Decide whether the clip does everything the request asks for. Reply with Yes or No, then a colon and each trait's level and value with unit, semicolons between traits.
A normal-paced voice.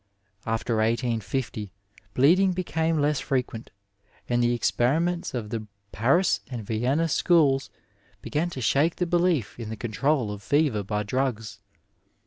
No: slow, 130 wpm